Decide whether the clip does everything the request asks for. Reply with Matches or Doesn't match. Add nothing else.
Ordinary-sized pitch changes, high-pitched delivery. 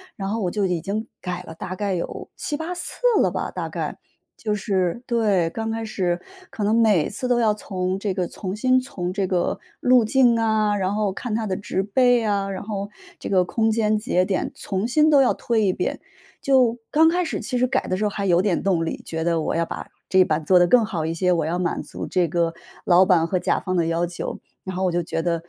Matches